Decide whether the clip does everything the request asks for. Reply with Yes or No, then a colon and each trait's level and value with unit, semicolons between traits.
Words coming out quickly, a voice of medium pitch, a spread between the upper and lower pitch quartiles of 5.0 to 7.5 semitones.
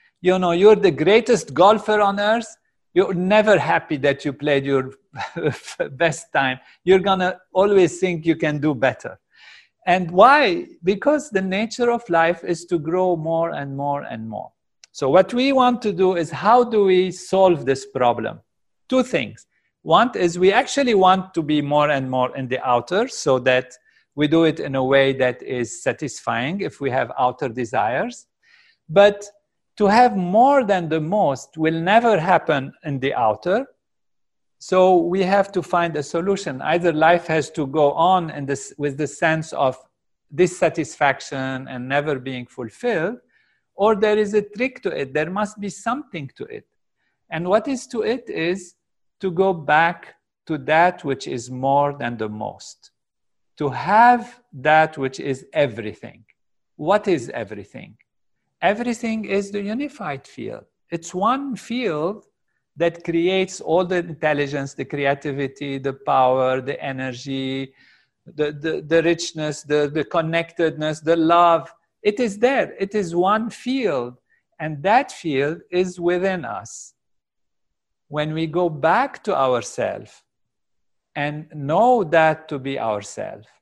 No: average, 155 wpm; medium, 165 Hz; wide, 5.6 semitones